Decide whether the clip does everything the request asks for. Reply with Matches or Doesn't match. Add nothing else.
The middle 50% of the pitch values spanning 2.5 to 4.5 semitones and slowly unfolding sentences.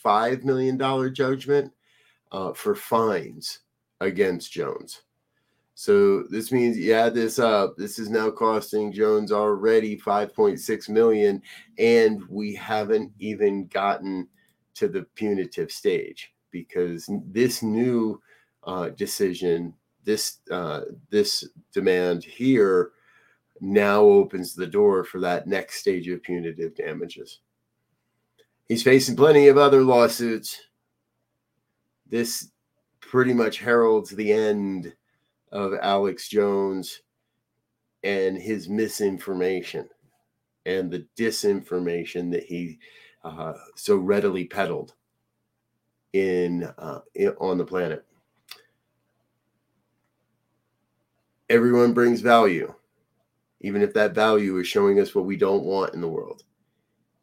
Doesn't match